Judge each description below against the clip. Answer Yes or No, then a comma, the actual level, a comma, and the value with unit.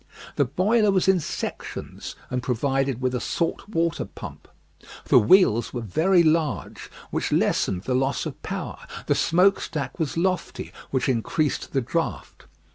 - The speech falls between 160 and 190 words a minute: No, average, 150 wpm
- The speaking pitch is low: No, medium, 150 Hz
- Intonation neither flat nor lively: No, wide, 5.8 semitones